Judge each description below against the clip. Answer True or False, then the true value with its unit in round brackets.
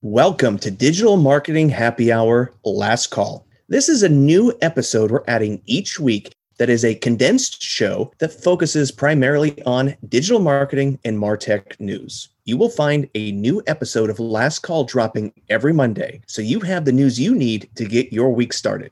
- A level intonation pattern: False (4.2 semitones)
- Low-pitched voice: True (130 Hz)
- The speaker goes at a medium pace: True (175 wpm)